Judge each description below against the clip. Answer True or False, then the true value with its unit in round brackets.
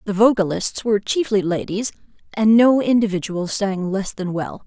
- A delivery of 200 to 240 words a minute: False (155 wpm)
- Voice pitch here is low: False (205 Hz)